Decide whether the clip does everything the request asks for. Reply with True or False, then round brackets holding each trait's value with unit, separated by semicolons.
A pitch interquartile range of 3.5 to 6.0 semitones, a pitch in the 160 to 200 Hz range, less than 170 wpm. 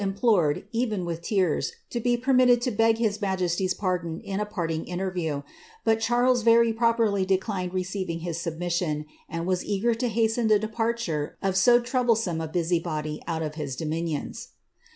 True (5.2 semitones; 190 Hz; 160 wpm)